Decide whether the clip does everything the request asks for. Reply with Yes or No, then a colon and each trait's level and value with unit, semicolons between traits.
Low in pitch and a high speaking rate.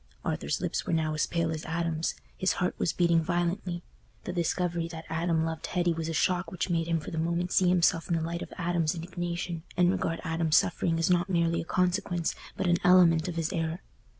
No: medium, 170 Hz; fast, 215 wpm